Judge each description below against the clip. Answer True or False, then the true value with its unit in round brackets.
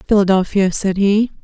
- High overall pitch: True (195 Hz)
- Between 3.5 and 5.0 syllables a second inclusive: False (5.2 syllables/s)